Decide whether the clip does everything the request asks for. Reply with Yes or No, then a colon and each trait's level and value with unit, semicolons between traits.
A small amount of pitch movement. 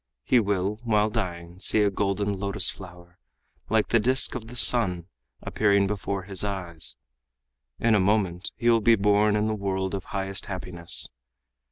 Yes: narrow, 2.3 semitones